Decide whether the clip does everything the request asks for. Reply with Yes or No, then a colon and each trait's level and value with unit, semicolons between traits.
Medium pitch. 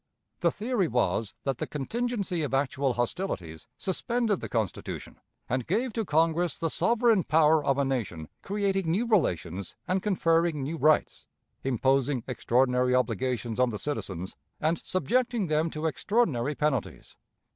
Yes: medium, 150 Hz